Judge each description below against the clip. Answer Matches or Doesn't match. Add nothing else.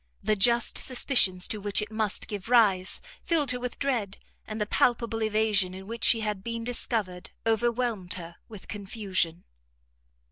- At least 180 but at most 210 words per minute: Doesn't match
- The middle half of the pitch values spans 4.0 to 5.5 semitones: Doesn't match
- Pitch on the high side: Matches